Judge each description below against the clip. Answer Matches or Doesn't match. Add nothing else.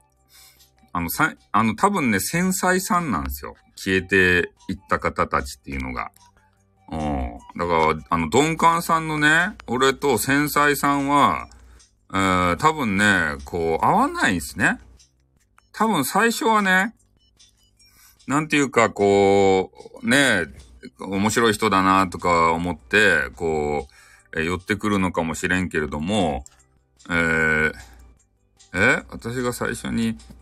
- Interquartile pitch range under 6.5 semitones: Doesn't match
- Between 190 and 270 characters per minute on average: Matches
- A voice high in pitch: Doesn't match